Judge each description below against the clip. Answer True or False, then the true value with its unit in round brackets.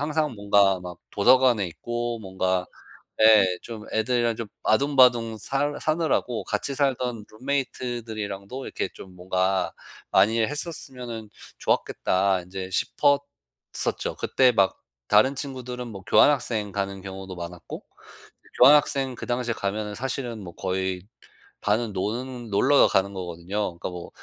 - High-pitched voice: False (110 Hz)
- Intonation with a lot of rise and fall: False (4.8 semitones)